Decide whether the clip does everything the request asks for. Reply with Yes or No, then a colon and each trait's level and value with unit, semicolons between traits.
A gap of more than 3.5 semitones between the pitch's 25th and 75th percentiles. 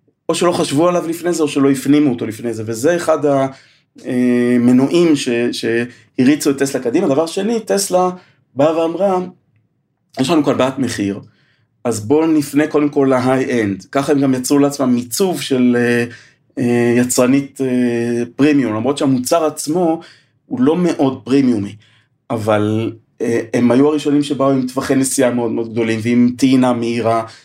Yes: average, 3.9 semitones